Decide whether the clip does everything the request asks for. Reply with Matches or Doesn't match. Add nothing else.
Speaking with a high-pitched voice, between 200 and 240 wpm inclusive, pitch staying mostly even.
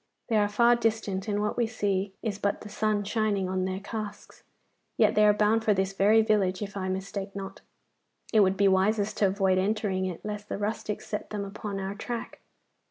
Matches